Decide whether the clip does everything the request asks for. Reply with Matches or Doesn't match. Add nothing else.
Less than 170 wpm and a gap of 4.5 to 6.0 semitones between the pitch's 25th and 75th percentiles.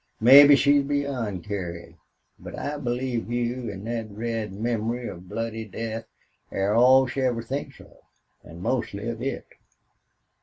Doesn't match